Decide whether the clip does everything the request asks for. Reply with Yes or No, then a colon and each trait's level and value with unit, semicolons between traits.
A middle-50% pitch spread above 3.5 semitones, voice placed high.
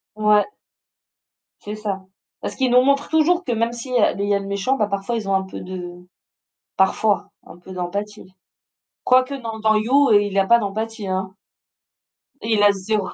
No: average, 3.2 semitones; high, 210 Hz